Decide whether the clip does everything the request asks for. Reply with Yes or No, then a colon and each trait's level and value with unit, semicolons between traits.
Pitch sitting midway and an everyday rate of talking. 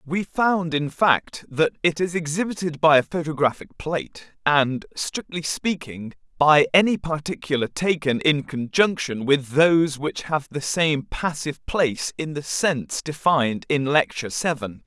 Yes: medium, 150 Hz; average, 145 wpm